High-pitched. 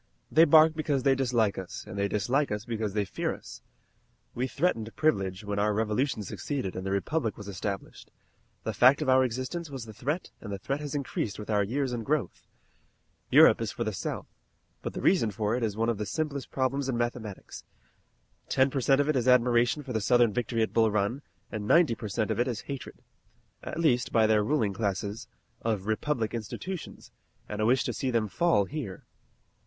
No: low, 120 Hz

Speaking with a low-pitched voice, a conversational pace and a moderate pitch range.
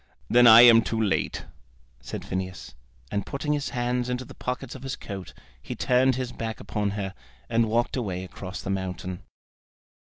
Yes: low, 115 Hz; average, 170 wpm; average, 4.3 semitones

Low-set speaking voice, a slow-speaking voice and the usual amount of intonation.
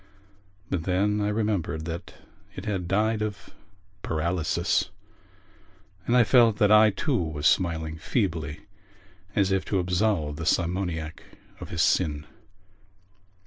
Yes: very low, 90 Hz; slow, 125 wpm; average, 4.5 semitones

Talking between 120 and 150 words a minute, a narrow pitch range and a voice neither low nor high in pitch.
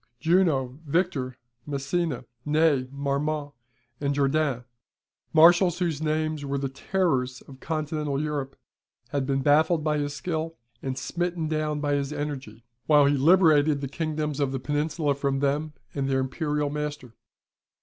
Yes: average, 140 wpm; narrow, 2.2 semitones; medium, 145 Hz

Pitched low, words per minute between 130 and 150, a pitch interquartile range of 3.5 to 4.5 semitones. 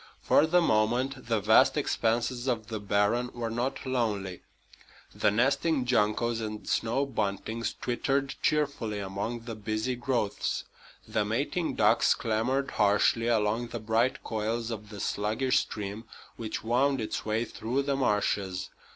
No: low, 115 Hz; average, 140 wpm; average, 3.1 semitones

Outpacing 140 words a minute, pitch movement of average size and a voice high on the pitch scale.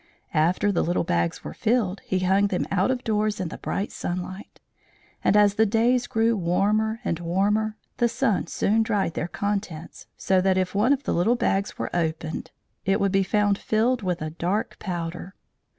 Yes: average, 185 wpm; average, 3.5 semitones; high, 195 Hz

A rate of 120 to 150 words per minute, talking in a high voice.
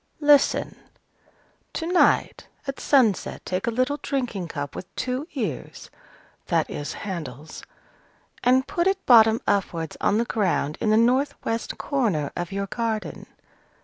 Yes: average, 140 wpm; high, 225 Hz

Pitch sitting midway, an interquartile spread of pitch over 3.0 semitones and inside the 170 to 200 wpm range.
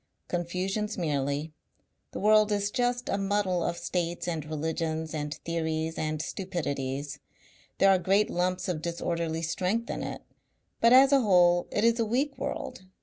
No: medium, 175 Hz; average, 4.4 semitones; average, 155 wpm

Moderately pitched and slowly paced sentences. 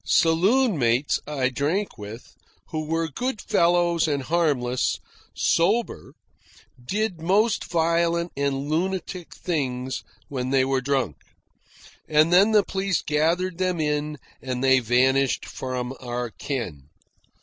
Yes: medium, 150 Hz; slow, 120 wpm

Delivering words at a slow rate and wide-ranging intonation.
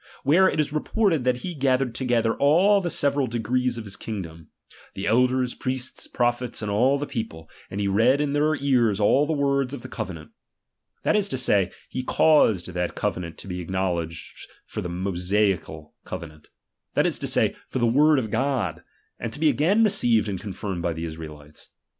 No: average, 190 wpm; wide, 6.8 semitones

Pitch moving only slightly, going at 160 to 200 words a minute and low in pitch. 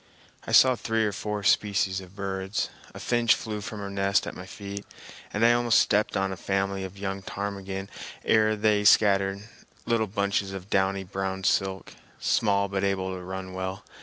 Yes: narrow, 1.5 semitones; average, 180 wpm; low, 100 Hz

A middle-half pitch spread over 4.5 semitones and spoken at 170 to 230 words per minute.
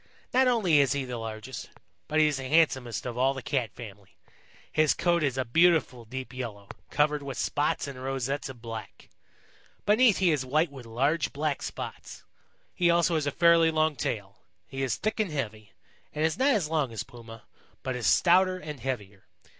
Yes: average, 5.0 semitones; average, 190 wpm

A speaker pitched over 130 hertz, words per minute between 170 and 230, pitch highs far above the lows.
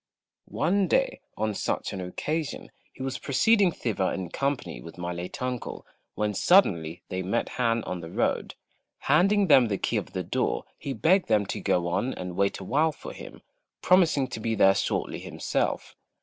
No: low, 115 Hz; average, 175 wpm; wide, 8.8 semitones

